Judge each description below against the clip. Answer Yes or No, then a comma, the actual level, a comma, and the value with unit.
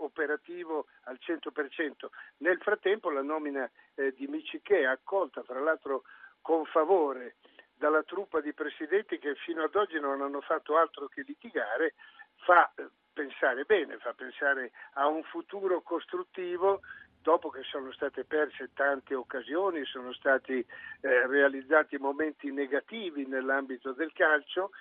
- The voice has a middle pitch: Yes, medium, 155 Hz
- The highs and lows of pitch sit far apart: Yes, wide, 7.0 semitones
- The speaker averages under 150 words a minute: Yes, average, 135 wpm